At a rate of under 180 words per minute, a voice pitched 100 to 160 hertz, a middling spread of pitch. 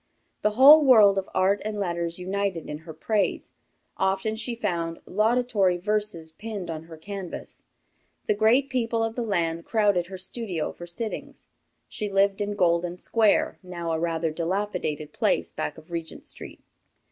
No: average, 160 wpm; high, 195 Hz; average, 4.0 semitones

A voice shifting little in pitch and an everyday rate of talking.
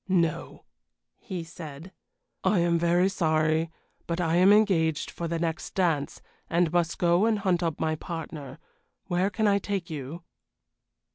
Yes: narrow, 2.3 semitones; average, 150 wpm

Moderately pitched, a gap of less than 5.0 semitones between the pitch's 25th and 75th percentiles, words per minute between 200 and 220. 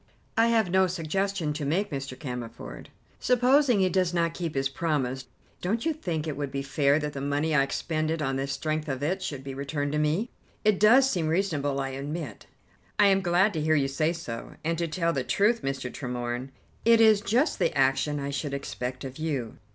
No: medium, 155 Hz; wide, 5.4 semitones; fast, 205 wpm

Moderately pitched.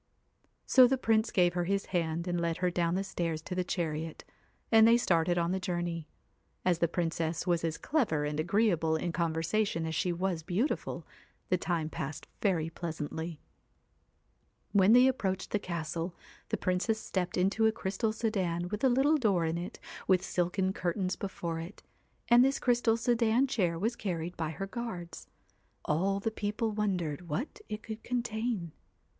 Yes: medium, 180 Hz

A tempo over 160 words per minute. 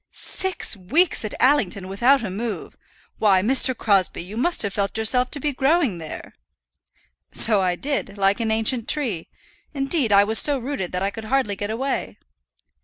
Yes: average, 175 wpm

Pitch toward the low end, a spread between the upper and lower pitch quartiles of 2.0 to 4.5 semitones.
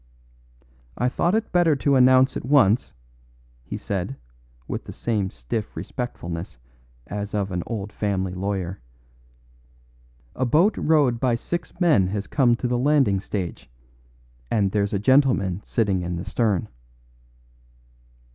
No: low, 110 Hz; average, 5.3 semitones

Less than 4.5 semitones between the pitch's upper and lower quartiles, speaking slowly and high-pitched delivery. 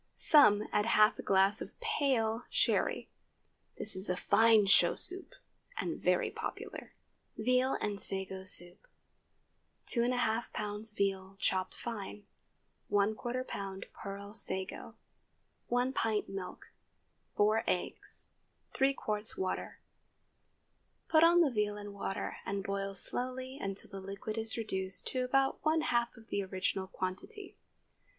Yes: average, 4.0 semitones; slow, 125 wpm; high, 210 Hz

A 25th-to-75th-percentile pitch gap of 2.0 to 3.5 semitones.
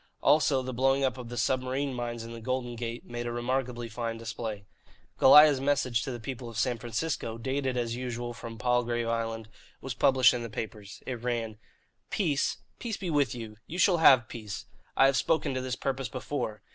Yes: narrow, 2.4 semitones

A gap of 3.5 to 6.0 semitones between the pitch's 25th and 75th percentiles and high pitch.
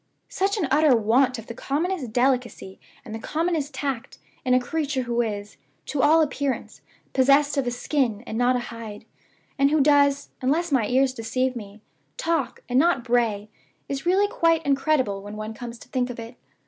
Yes: average, 4.0 semitones; very high, 260 Hz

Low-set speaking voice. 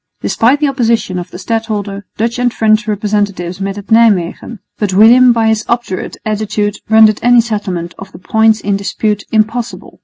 No: high, 215 Hz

